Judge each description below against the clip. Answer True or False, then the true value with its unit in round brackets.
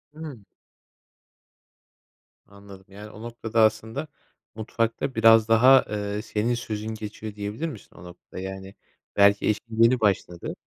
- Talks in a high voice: False (110 Hz)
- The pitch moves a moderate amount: False (2.2 semitones)